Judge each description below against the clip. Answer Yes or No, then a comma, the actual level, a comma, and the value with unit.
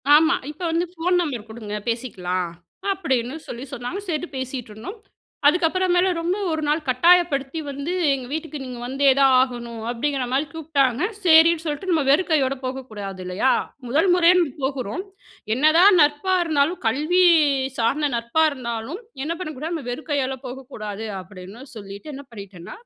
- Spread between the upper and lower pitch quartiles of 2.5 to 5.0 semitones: No, wide, 5.4 semitones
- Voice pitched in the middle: No, very high, 275 Hz